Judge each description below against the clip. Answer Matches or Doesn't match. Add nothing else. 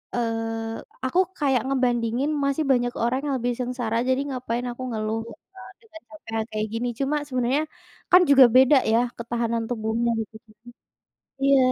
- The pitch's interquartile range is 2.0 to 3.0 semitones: Matches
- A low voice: Doesn't match